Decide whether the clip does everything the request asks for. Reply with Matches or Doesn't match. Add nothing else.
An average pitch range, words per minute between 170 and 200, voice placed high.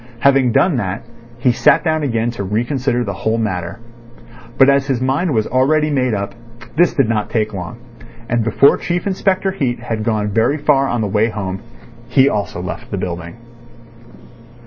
Doesn't match